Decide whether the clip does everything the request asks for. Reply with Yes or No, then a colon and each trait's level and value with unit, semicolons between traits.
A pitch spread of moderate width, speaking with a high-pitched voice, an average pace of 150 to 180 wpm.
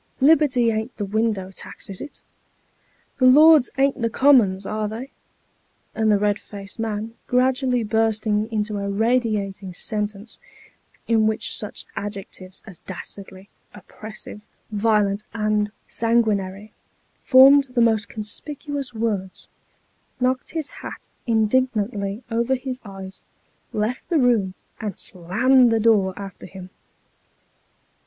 No: average, 3.7 semitones; high, 220 Hz; slow, 135 wpm